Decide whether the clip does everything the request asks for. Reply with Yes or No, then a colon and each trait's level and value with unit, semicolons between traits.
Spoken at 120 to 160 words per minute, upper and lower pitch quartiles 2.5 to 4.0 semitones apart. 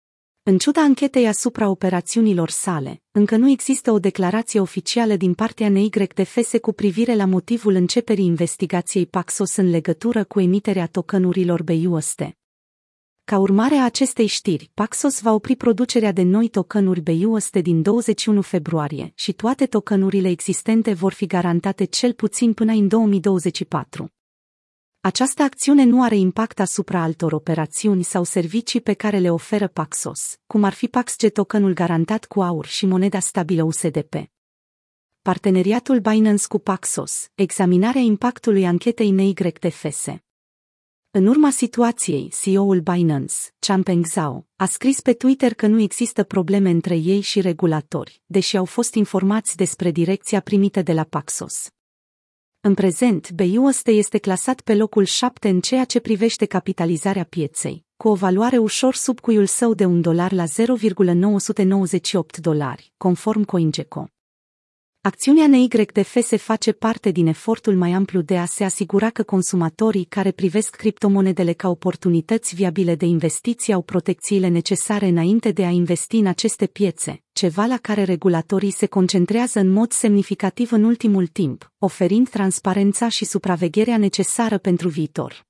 Yes: average, 140 wpm; average, 3.5 semitones